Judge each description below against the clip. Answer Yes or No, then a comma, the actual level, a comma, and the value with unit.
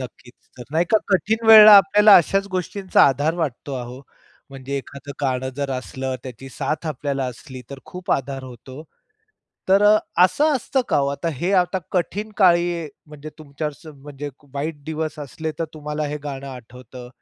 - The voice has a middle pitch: Yes, medium, 150 Hz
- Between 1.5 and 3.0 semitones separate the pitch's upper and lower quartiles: No, average, 5.1 semitones